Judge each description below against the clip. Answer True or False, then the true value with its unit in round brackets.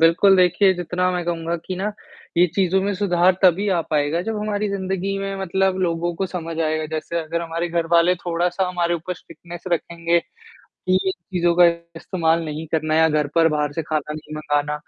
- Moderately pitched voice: True (170 Hz)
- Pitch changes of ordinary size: False (2.2 semitones)